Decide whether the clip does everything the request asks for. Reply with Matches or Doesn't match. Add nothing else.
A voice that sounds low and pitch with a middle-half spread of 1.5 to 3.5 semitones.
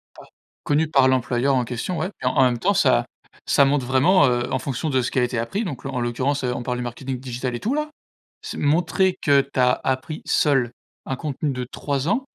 Matches